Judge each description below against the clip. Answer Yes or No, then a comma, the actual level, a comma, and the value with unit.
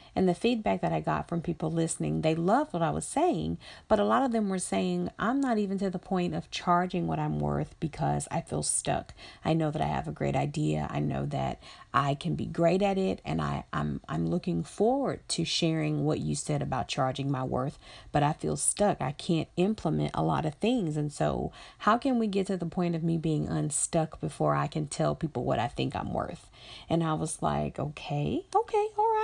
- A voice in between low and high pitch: Yes, medium, 165 Hz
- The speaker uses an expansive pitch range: Yes, wide, 6.8 semitones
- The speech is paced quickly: Yes, fast, 230 wpm